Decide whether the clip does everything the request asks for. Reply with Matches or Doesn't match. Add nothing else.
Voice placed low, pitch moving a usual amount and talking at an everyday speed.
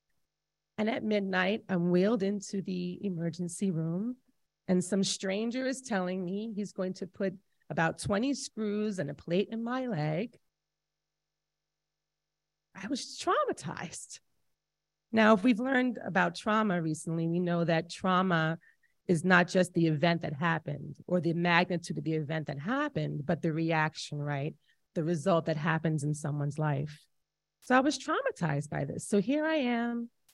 Doesn't match